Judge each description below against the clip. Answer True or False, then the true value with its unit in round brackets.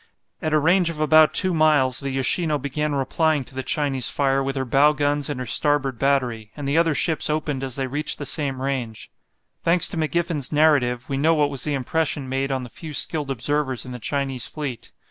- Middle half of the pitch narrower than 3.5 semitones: True (2.6 semitones)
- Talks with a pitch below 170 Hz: True (140 Hz)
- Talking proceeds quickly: True (215 wpm)